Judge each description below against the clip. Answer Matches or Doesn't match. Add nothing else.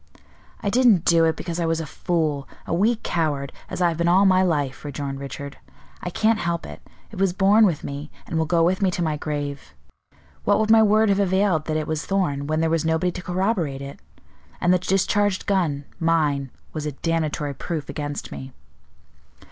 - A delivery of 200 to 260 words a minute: Matches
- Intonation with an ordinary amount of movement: Matches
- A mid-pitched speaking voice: Matches